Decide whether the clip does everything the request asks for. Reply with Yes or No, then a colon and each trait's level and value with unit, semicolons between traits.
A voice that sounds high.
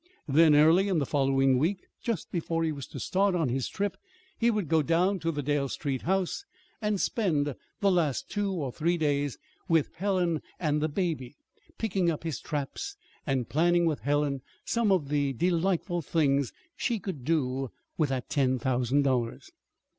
No: medium, 160 Hz